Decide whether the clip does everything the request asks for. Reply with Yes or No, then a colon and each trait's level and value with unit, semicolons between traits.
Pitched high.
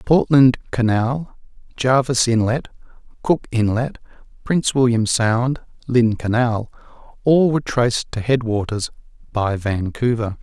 No: low, 120 Hz